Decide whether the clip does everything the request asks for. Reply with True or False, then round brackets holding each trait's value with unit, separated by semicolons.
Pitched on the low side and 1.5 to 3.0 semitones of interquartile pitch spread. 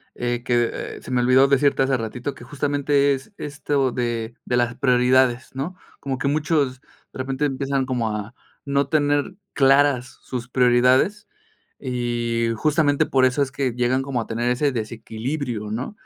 True (130 Hz; 2.6 semitones)